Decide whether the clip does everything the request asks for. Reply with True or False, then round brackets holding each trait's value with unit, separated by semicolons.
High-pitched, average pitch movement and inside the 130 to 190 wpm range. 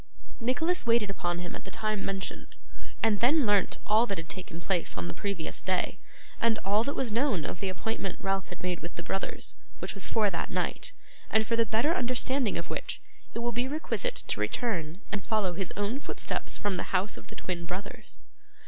False (205 Hz; 4.0 semitones; 205 wpm)